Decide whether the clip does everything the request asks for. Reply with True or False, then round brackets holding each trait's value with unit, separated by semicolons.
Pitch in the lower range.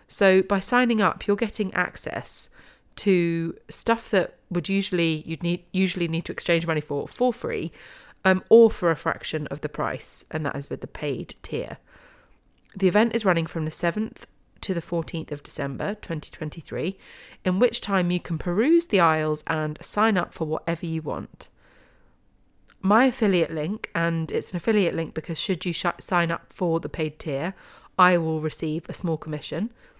False (175 Hz)